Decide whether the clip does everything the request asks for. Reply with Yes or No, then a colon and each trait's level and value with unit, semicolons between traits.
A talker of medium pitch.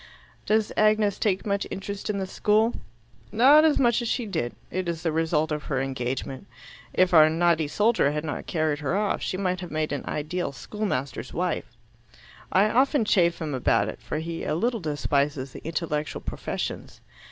Yes: medium, 170 Hz